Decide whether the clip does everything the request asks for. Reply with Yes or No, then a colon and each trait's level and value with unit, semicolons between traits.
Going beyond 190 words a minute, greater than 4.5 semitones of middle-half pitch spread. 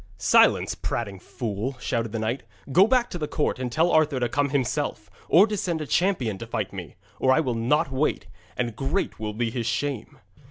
Yes: fast, 205 wpm; wide, 5.4 semitones